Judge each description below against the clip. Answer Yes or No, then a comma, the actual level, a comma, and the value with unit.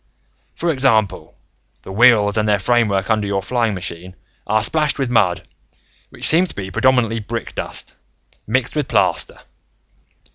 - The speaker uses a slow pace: No, average, 145 wpm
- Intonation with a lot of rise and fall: No, average, 4.0 semitones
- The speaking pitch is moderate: No, low, 110 Hz